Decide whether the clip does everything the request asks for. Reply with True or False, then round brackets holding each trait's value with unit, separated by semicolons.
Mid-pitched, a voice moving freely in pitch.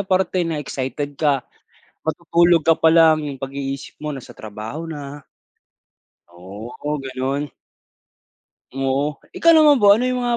False (150 Hz; 3.9 semitones)